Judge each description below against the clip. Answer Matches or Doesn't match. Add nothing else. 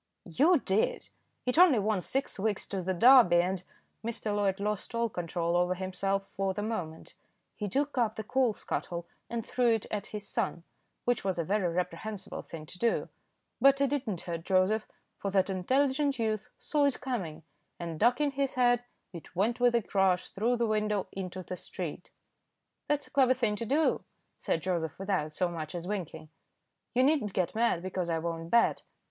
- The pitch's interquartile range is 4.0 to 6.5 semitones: Matches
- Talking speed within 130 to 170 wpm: Doesn't match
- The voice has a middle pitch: Doesn't match